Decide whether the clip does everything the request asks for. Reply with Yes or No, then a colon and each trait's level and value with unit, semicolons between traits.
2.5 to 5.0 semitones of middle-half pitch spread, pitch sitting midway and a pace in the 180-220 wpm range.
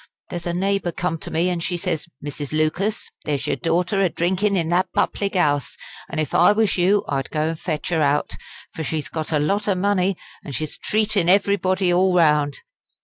Yes: average, 3.8 semitones; medium, 175 Hz; average, 200 wpm